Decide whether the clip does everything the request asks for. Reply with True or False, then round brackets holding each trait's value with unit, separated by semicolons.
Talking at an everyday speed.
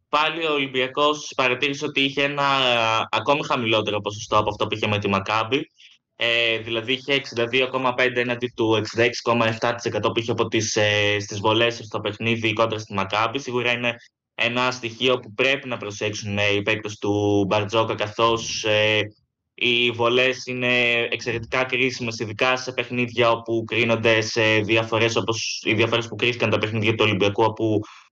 True (155 wpm)